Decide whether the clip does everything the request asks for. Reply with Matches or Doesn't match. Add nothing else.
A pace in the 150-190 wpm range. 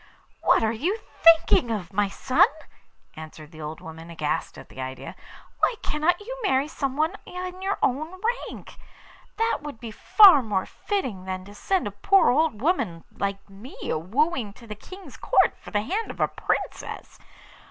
Matches